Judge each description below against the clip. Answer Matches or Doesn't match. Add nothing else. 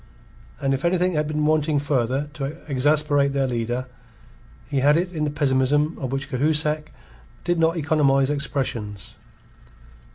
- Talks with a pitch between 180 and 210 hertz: Doesn't match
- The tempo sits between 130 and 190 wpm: Matches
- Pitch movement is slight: Matches